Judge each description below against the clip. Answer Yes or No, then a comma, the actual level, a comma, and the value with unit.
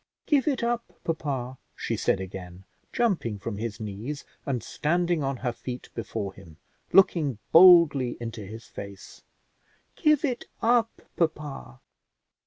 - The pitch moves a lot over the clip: Yes, wide, 8.3 semitones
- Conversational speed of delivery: No, slow, 130 wpm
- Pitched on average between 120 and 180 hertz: Yes, low, 135 Hz